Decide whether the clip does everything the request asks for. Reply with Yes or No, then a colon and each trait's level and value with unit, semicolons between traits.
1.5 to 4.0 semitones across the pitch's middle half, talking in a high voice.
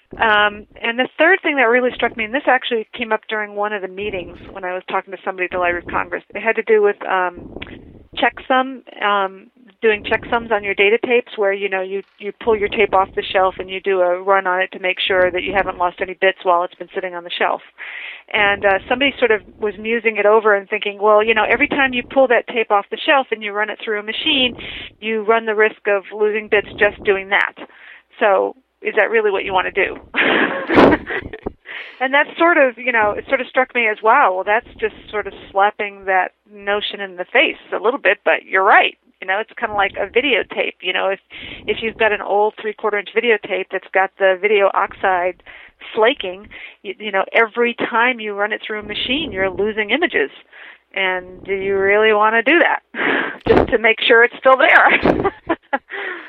Yes: average, 3.4 semitones; high, 210 Hz